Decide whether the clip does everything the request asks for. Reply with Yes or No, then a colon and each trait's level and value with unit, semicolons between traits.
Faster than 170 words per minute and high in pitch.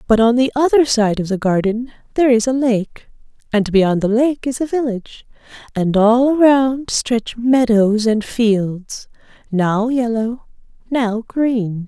No: average, 150 wpm; high, 235 Hz